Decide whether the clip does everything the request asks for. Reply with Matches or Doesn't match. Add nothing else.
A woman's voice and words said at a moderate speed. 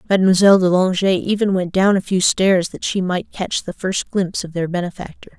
Doesn't match